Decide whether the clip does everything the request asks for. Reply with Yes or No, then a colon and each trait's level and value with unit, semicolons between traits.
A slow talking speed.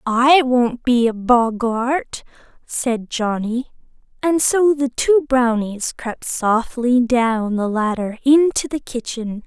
Yes: slow, 125 wpm